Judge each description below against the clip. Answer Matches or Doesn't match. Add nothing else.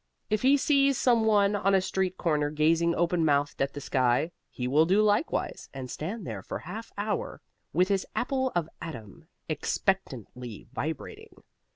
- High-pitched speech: Doesn't match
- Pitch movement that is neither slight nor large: Doesn't match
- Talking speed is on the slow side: Doesn't match